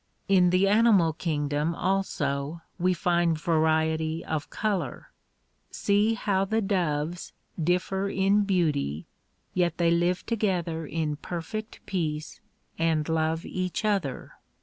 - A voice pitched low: No, medium, 170 Hz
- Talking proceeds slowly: Yes, slow, 115 wpm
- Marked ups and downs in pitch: No, average, 3.4 semitones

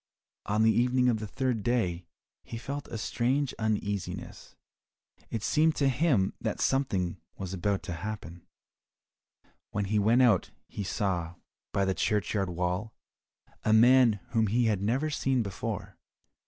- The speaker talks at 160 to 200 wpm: No, average, 145 wpm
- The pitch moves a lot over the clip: No, average, 4.3 semitones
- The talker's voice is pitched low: Yes, low, 110 Hz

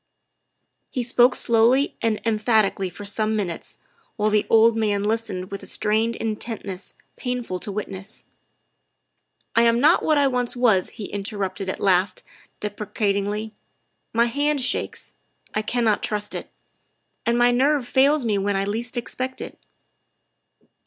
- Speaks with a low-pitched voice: No, high, 220 Hz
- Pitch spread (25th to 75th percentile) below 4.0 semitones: Yes, average, 3.0 semitones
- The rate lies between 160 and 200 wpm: No, average, 145 wpm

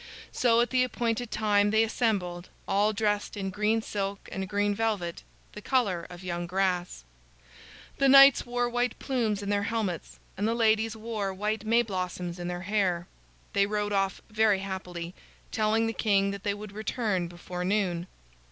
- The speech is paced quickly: No, average, 170 wpm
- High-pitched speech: Yes, high, 205 Hz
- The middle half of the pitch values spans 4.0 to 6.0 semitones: No, average, 3.0 semitones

